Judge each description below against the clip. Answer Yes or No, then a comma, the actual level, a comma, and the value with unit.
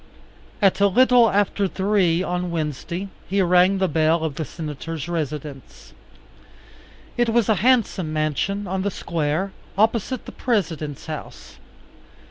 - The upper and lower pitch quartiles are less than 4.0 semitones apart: No, average, 4.4 semitones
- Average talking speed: No, slow, 130 wpm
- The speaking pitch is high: No, medium, 180 Hz